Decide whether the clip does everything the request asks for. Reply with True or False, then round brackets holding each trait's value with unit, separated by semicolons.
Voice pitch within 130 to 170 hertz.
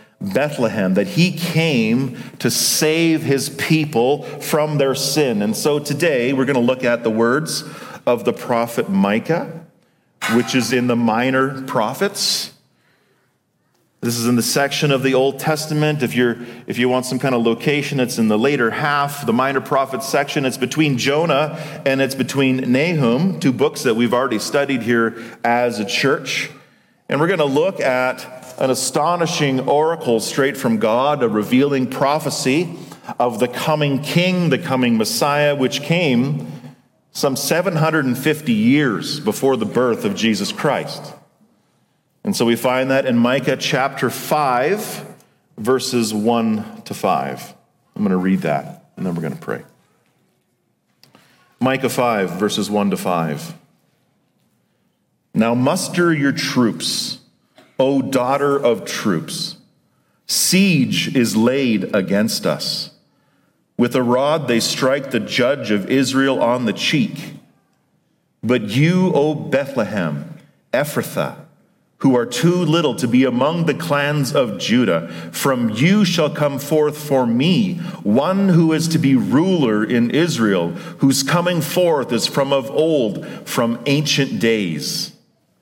True (135 Hz)